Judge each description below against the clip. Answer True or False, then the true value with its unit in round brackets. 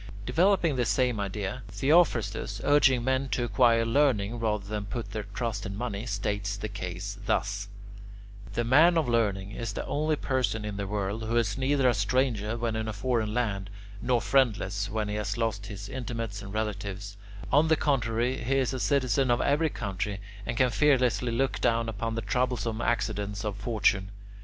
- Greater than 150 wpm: True (180 wpm)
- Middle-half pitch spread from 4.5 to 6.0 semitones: False (3.8 semitones)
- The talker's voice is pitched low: True (115 Hz)